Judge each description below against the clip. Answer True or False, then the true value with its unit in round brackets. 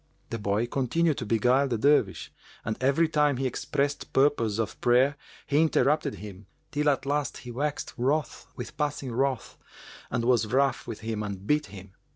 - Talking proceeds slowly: False (175 wpm)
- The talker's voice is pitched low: True (130 Hz)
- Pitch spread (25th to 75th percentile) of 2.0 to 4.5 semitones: True (4.2 semitones)